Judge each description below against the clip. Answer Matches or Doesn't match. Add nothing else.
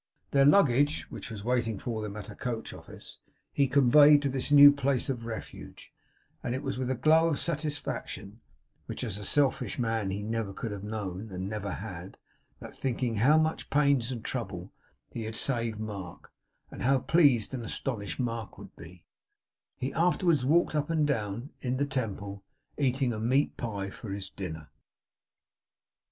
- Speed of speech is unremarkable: Matches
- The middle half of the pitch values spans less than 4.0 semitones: Doesn't match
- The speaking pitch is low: Matches